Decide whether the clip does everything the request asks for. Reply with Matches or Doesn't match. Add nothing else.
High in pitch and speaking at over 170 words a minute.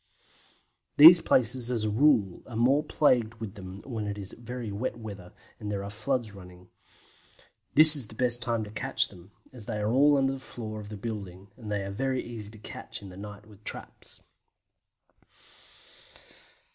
Doesn't match